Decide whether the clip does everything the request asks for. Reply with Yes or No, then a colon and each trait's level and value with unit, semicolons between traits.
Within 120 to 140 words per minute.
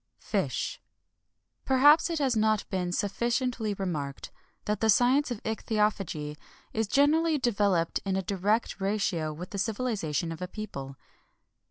Yes: slow, 135 wpm